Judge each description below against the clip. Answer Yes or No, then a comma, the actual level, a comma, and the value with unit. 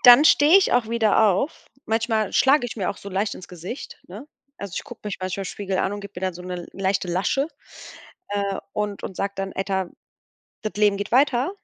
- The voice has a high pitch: Yes, high, 200 Hz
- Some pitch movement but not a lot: Yes, average, 3.5 semitones